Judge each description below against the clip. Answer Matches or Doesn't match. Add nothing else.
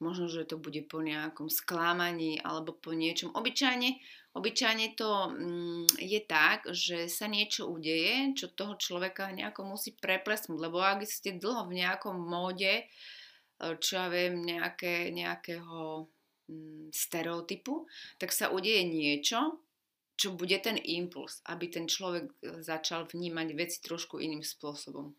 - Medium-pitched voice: Matches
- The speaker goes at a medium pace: Matches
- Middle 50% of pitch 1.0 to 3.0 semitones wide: Doesn't match